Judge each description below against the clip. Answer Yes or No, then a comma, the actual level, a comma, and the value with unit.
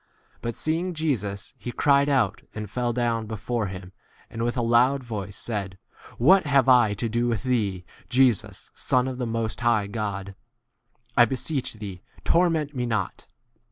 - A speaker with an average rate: Yes, average, 160 wpm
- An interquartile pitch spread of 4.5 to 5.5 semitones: No, average, 3.7 semitones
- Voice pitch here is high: No, low, 120 Hz